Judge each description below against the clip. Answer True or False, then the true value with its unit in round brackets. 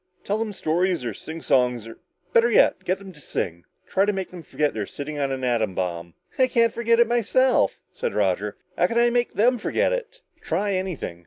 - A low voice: False (190 Hz)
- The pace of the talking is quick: True (215 wpm)